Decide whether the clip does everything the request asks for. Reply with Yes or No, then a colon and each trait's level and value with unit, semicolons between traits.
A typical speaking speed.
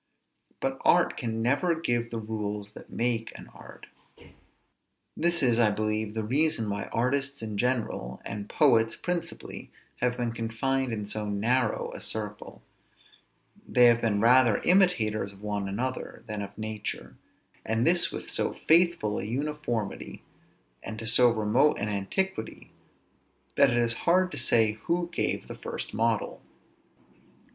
Yes: average, 145 wpm